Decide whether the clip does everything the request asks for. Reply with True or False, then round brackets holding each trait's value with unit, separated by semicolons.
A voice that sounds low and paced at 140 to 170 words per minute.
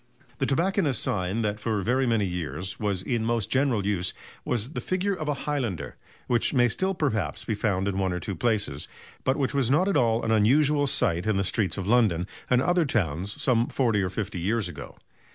False (110 Hz; 205 wpm)